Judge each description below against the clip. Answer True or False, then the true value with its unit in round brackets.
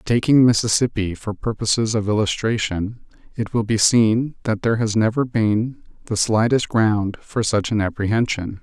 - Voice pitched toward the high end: False (110 Hz)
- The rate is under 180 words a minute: True (155 wpm)